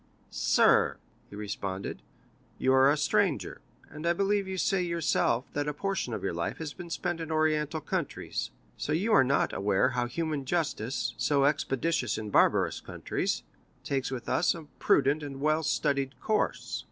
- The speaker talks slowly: No, average, 165 wpm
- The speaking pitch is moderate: Yes, medium, 145 Hz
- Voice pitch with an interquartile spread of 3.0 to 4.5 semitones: Yes, average, 4.1 semitones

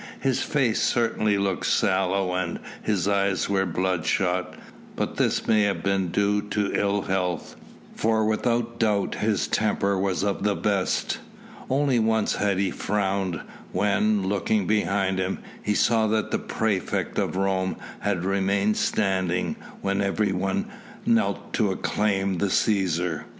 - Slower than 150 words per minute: Yes, average, 140 wpm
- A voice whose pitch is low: Yes, low, 100 Hz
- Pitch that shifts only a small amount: Yes, narrow, 2.1 semitones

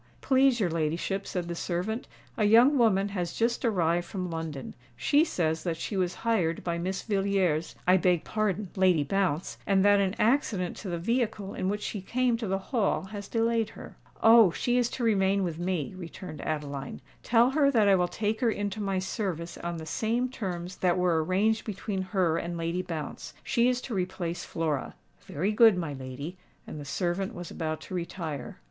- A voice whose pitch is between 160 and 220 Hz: Yes, high, 190 Hz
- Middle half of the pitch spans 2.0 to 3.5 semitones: No, average, 4.3 semitones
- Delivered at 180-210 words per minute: Yes, average, 185 wpm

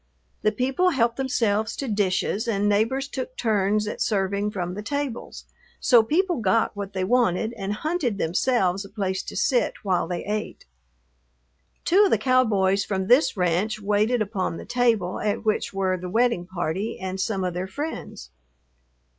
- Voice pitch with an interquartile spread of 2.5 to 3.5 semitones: No, average, 4.2 semitones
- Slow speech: No, average, 165 wpm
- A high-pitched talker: Yes, high, 210 Hz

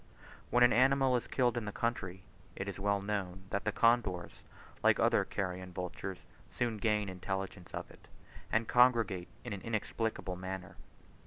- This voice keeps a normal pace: Yes, average, 160 wpm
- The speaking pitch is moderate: No, low, 100 Hz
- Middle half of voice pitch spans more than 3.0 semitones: Yes, average, 3.8 semitones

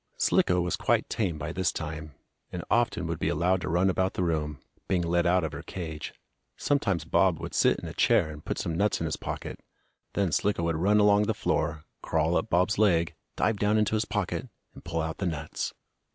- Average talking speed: No, fast, 220 wpm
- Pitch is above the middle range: No, very low, 90 Hz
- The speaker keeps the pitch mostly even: No, average, 3.9 semitones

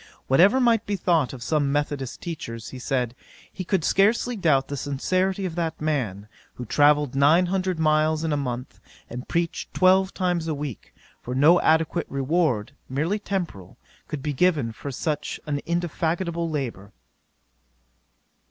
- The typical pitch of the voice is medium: Yes, medium, 155 Hz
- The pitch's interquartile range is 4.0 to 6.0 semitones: Yes, average, 4.6 semitones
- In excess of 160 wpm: No, average, 150 wpm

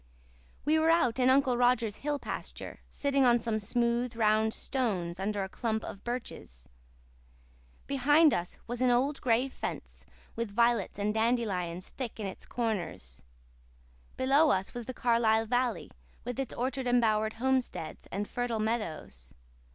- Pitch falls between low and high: No, high, 235 Hz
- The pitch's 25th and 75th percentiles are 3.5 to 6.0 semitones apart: No, average, 3.1 semitones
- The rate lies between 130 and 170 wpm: Yes, average, 145 wpm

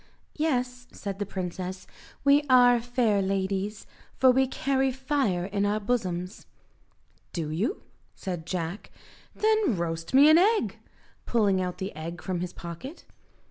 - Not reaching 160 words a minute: Yes, average, 140 wpm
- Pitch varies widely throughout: Yes, wide, 6.2 semitones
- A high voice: Yes, high, 205 Hz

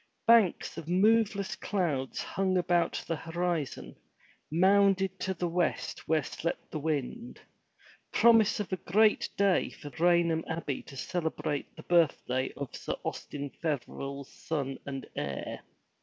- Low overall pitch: No, medium, 170 Hz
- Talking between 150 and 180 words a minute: No, slow, 135 wpm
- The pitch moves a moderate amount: Yes, average, 4.6 semitones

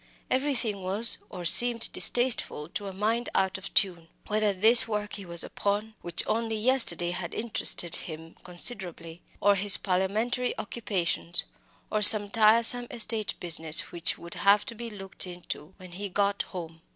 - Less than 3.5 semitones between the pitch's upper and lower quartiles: No, average, 4.1 semitones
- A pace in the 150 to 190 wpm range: Yes, average, 155 wpm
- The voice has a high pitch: Yes, high, 200 Hz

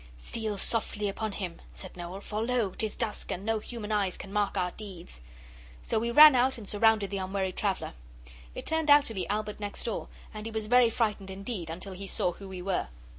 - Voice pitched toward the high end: Yes, high, 210 Hz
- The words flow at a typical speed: No, fast, 215 wpm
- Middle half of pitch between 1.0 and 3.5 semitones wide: Yes, average, 2.7 semitones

